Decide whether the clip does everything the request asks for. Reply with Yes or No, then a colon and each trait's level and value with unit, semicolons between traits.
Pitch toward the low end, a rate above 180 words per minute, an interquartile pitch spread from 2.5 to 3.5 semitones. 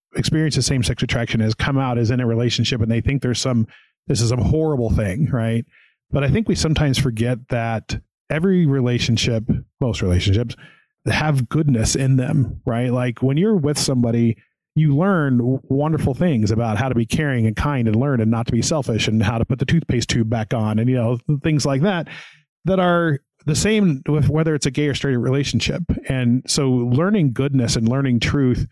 No: low, 130 Hz; average, 200 wpm; average, 4.0 semitones